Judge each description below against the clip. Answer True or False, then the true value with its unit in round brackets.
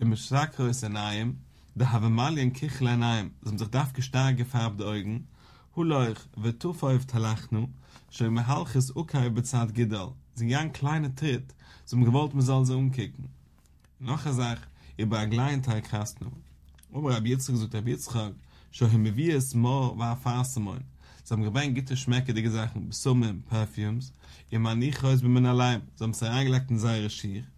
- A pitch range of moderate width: True (3.0 semitones)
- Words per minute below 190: True (170 wpm)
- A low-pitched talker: True (120 Hz)